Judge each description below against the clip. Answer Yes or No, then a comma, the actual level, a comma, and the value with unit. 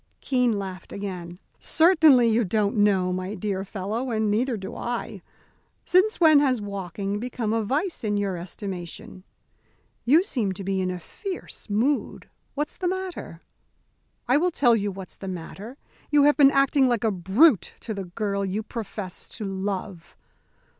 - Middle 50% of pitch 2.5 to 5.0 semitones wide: No, wide, 5.4 semitones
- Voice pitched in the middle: No, high, 210 Hz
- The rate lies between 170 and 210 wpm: No, average, 160 wpm